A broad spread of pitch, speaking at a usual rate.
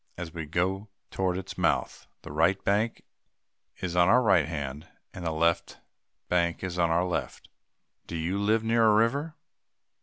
No: average, 3.7 semitones; average, 170 wpm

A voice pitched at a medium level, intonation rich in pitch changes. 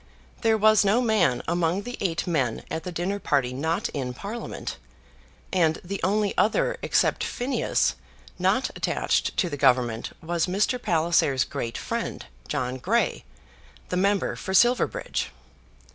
Yes: medium, 175 Hz; wide, 6.6 semitones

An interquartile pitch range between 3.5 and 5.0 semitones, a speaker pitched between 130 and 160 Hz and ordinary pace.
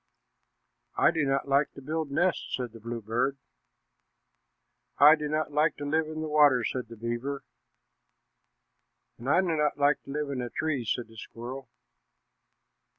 Yes: average, 3.8 semitones; medium, 140 Hz; average, 160 wpm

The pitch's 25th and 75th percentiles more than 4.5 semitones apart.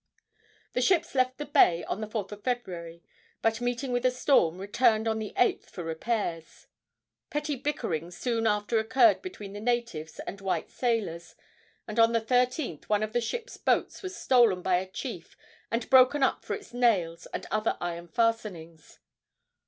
Yes: average, 5.0 semitones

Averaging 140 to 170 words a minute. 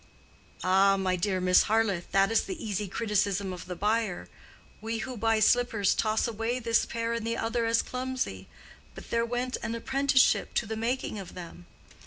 No: average, 180 wpm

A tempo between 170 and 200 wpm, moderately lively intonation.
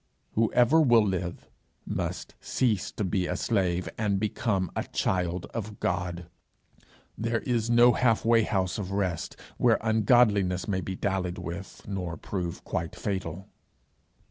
No: average, 140 wpm; average, 3.7 semitones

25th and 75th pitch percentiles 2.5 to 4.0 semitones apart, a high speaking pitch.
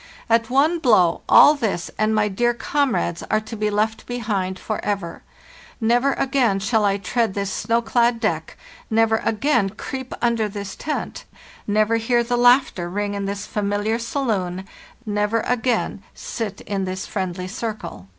Yes: average, 3.1 semitones; high, 220 Hz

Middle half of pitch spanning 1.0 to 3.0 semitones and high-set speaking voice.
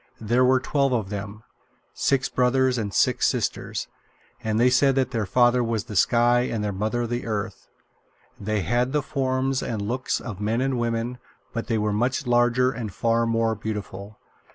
No: average, 2.7 semitones; low, 120 Hz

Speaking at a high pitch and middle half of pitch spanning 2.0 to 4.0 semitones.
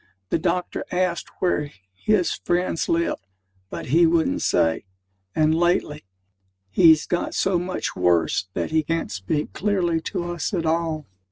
No: medium, 165 Hz; narrow, 2.4 semitones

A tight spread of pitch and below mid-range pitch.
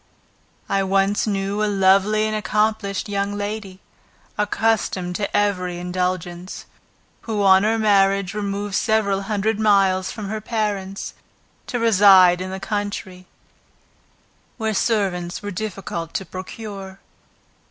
No: narrow, 2.0 semitones; high, 200 Hz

